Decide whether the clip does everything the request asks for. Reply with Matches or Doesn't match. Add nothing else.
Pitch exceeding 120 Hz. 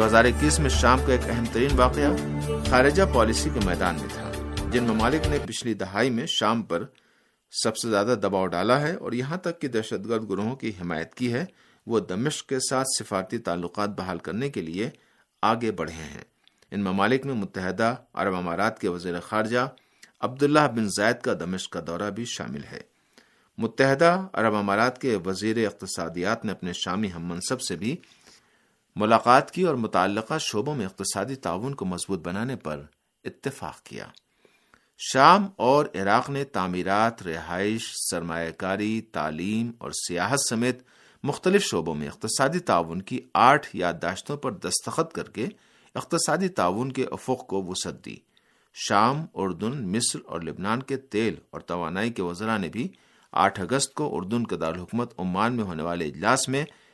Doesn't match